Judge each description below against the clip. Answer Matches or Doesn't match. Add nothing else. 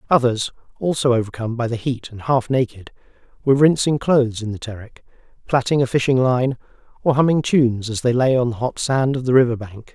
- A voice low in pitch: Matches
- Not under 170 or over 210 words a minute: Matches